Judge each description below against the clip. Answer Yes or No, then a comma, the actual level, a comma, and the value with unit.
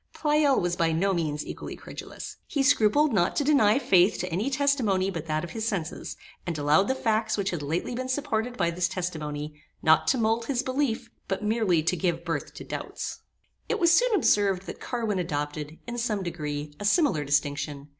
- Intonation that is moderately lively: No, wide, 6.9 semitones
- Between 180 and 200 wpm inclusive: Yes, average, 195 wpm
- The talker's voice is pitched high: Yes, high, 195 Hz